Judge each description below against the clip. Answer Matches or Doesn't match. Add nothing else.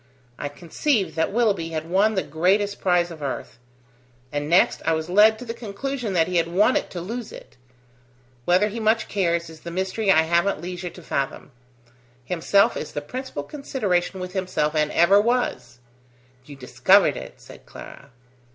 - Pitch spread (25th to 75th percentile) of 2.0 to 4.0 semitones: Doesn't match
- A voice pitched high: Doesn't match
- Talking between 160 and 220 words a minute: Matches